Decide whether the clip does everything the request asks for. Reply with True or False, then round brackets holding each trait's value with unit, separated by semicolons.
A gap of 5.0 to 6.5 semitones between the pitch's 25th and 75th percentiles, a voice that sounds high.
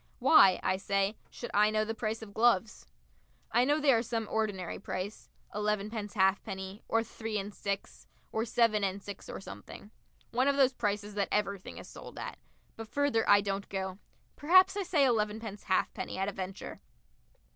False (2.6 semitones; 210 Hz)